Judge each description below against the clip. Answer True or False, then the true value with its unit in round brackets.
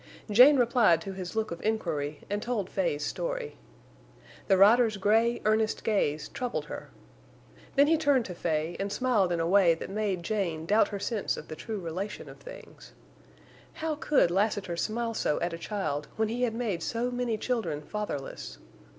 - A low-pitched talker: False (210 Hz)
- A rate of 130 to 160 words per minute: False (175 wpm)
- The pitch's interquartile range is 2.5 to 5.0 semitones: False (5.4 semitones)